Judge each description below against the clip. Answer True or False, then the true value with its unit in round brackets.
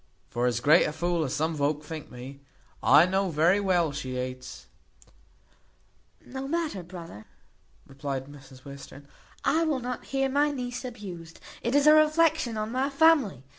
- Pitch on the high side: False (175 Hz)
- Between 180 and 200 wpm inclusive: False (165 wpm)